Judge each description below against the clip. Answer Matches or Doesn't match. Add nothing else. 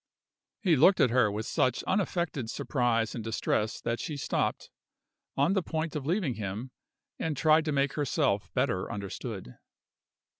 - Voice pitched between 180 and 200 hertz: Doesn't match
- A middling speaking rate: Matches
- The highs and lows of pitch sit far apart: Matches